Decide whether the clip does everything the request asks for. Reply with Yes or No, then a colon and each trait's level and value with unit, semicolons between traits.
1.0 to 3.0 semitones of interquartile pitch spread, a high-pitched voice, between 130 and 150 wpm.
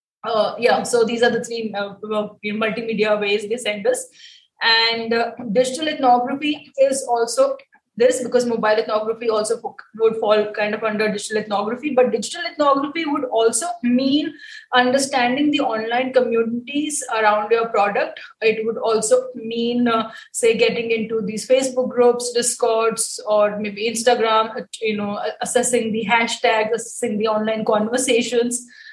Yes: narrow, 2.5 semitones; high, 235 Hz; average, 145 wpm